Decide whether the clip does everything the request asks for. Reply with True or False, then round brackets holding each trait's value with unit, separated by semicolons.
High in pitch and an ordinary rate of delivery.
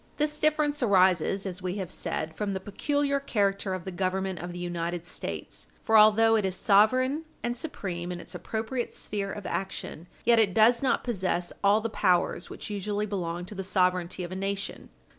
True (195 Hz; 190 wpm)